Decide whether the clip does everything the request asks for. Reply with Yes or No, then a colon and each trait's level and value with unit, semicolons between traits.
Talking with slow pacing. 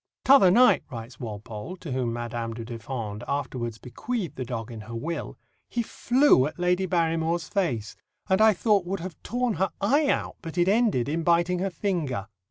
No: average, 180 wpm